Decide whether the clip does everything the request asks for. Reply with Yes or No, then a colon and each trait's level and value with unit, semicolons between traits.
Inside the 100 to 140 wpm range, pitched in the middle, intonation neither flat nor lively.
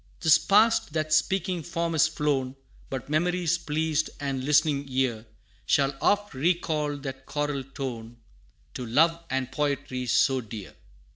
Yes: slow, 135 wpm; medium, 145 Hz; average, 3.4 semitones